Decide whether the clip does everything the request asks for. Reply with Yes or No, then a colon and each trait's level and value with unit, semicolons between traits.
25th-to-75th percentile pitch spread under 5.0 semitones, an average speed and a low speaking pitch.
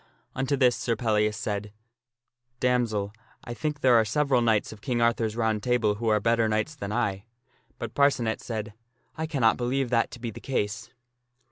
Yes: average, 2.7 semitones; average, 190 wpm; low, 115 Hz